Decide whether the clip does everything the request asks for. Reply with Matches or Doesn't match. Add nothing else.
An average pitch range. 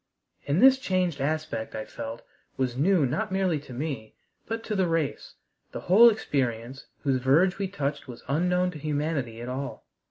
Doesn't match